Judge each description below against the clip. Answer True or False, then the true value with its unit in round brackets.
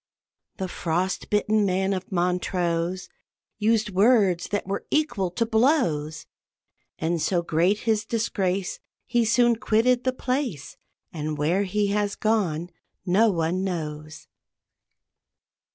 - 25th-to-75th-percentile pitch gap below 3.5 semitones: False (4.2 semitones)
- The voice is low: False (190 Hz)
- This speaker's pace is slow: True (120 wpm)